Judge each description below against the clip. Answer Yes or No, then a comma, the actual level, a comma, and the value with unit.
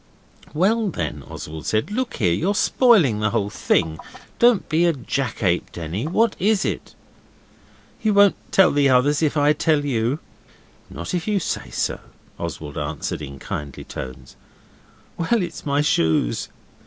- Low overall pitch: No, medium, 145 Hz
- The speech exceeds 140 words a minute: Yes, average, 150 wpm